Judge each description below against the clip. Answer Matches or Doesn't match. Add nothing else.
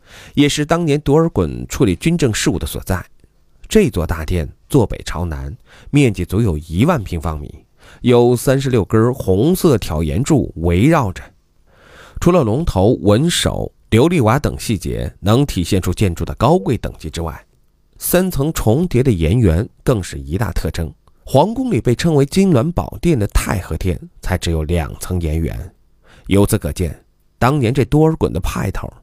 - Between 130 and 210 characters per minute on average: Doesn't match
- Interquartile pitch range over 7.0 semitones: Matches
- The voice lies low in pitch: Matches